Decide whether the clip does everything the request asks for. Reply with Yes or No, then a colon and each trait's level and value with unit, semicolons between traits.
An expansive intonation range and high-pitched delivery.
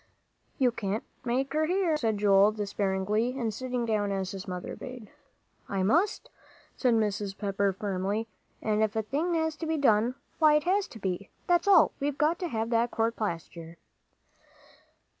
Yes: wide, 6.2 semitones; high, 225 Hz